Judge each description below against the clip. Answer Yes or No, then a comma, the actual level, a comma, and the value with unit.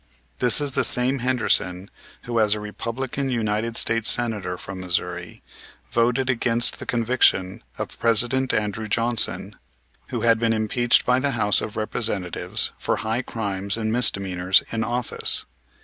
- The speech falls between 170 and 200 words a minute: No, average, 145 wpm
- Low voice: Yes, low, 115 Hz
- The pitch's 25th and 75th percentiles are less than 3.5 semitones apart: Yes, average, 2.7 semitones